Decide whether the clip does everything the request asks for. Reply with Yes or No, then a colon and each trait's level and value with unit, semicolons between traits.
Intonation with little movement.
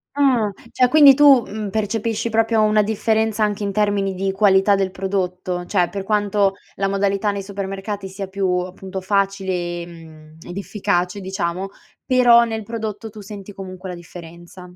Yes: narrow, 2.3 semitones